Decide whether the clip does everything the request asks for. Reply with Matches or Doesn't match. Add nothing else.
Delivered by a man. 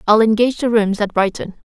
Doesn't match